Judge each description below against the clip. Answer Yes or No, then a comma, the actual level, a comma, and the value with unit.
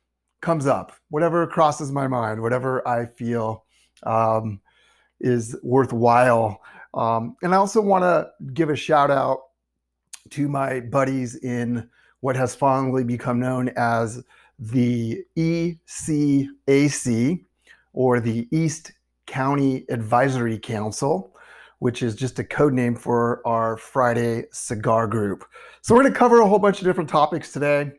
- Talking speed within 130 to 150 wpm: Yes, slow, 135 wpm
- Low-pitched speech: Yes, low, 125 Hz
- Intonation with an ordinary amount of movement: Yes, average, 3.7 semitones